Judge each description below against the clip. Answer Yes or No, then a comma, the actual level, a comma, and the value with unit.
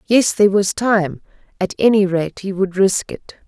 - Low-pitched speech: No, high, 195 Hz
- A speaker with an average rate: Yes, average, 190 wpm